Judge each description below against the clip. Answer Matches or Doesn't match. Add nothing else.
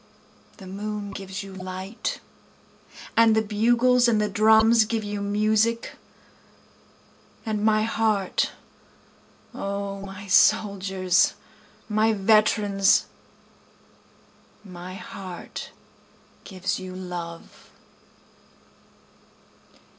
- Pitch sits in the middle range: Doesn't match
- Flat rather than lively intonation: Matches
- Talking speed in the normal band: Doesn't match